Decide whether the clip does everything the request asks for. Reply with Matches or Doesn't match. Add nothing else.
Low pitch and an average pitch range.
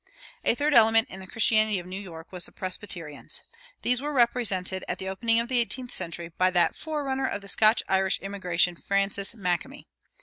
Doesn't match